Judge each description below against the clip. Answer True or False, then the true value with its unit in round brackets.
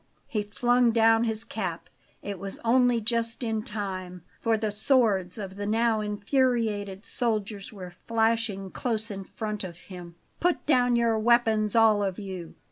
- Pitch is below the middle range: False (215 Hz)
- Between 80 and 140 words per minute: False (155 wpm)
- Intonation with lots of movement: False (2.6 semitones)